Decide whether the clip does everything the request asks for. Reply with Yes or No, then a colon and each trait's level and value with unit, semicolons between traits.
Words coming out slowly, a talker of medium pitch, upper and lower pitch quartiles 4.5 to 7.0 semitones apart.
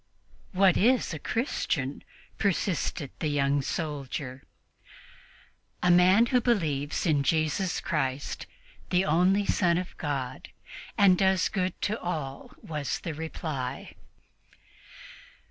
Yes: slow, 110 wpm; medium, 160 Hz; average, 4.8 semitones